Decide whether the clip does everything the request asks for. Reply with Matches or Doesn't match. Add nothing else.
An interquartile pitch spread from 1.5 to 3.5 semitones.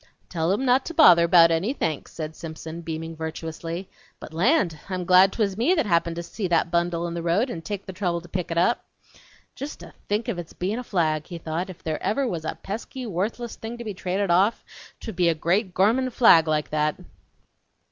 Doesn't match